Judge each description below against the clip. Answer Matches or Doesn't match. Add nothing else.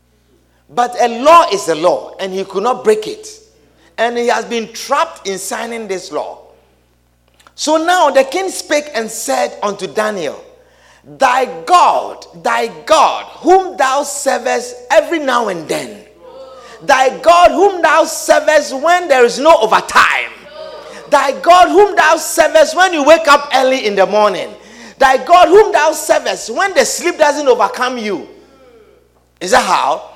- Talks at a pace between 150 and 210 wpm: Matches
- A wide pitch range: Matches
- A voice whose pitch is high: Matches